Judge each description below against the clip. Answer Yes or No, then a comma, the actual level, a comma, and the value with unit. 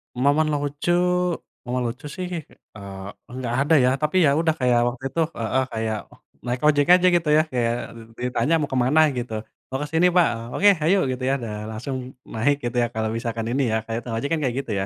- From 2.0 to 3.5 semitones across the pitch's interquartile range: No, average, 4.2 semitones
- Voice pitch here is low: Yes, low, 130 Hz